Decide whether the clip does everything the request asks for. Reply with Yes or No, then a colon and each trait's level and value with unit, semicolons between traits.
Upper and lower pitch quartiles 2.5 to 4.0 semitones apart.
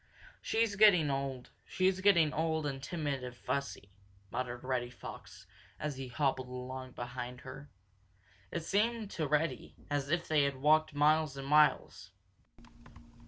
Yes: average, 3.5 semitones